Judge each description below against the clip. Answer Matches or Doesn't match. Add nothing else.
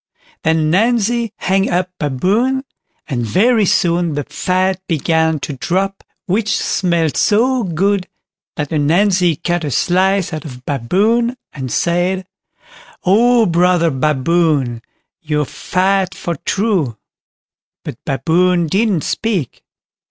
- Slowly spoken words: Matches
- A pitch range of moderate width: Matches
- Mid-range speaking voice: Matches